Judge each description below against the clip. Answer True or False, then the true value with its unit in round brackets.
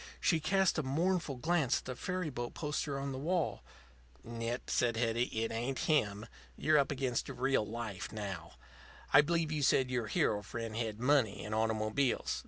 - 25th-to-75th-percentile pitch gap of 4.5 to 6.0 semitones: True (4.8 semitones)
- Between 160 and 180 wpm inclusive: True (175 wpm)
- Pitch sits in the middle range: False (125 Hz)